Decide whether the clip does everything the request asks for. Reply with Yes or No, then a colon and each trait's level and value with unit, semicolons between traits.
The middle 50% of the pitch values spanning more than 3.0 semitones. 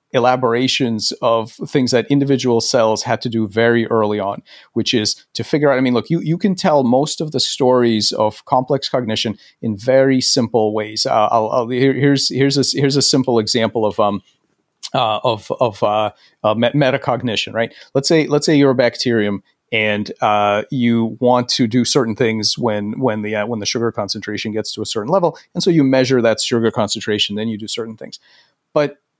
Yes: average, 3.7 semitones